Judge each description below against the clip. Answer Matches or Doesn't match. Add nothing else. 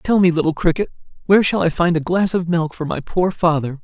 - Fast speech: Matches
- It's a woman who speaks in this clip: Doesn't match